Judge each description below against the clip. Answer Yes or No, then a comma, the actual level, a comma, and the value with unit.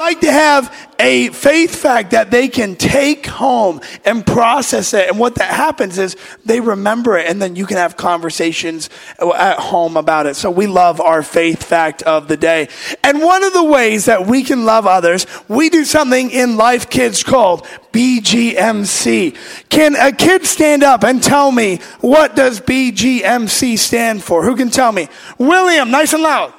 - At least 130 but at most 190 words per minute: Yes, average, 180 wpm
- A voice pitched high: Yes, high, 235 Hz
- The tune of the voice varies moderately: No, wide, 7.2 semitones